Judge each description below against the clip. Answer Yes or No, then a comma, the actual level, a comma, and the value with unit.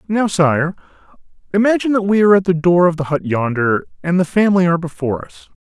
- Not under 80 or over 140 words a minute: No, average, 200 wpm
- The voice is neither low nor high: Yes, medium, 170 Hz